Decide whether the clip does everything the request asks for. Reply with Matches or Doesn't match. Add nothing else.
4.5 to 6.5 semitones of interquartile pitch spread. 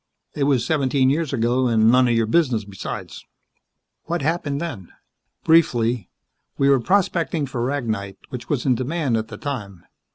Doesn't match